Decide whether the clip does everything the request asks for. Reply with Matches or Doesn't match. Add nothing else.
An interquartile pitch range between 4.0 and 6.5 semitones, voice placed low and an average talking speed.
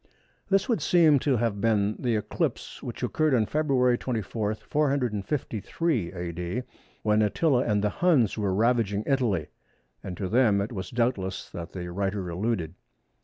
Matches